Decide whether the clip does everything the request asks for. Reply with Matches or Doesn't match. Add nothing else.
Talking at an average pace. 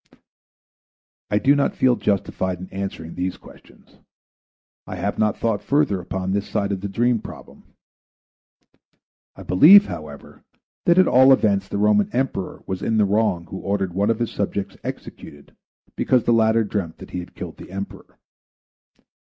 Matches